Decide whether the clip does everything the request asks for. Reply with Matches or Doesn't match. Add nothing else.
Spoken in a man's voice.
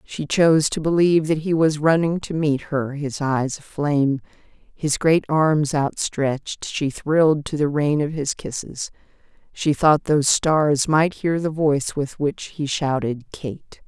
Doesn't match